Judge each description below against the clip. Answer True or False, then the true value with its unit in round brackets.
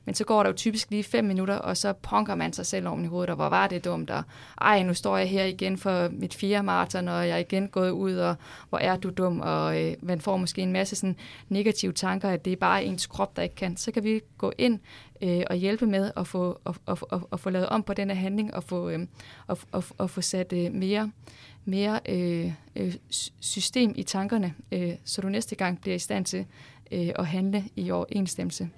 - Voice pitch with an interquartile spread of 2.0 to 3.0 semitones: True (2.4 semitones)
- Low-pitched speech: False (185 Hz)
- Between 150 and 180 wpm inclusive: False (225 wpm)